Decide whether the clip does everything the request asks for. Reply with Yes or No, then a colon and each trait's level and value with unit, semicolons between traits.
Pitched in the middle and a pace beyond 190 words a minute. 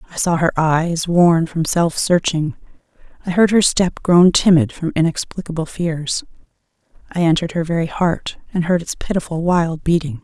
No: medium, 170 Hz; average, 165 wpm